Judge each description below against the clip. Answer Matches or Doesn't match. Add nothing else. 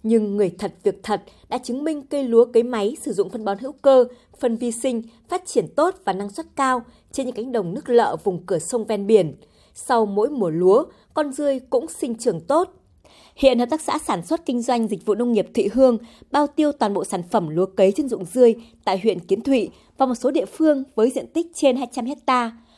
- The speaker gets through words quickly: Doesn't match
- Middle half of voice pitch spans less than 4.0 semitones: Doesn't match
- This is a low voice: Doesn't match